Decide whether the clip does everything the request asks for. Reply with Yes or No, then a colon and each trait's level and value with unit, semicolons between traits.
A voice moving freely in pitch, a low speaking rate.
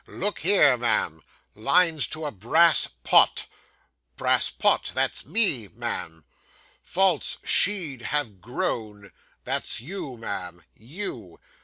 Yes: wide, 8.4 semitones; slow, 110 wpm